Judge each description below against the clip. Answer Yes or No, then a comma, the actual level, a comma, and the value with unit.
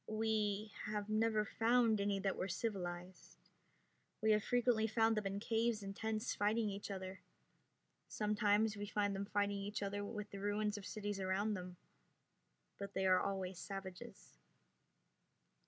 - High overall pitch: Yes, high, 205 Hz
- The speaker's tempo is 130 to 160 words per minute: Yes, average, 150 wpm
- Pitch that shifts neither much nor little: No, narrow, 1.7 semitones